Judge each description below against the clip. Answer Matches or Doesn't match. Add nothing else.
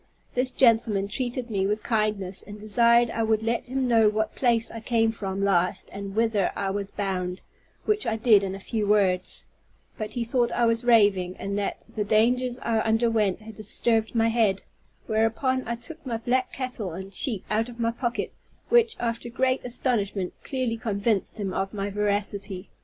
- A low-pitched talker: Doesn't match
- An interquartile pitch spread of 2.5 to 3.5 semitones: Matches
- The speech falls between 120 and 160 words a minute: Doesn't match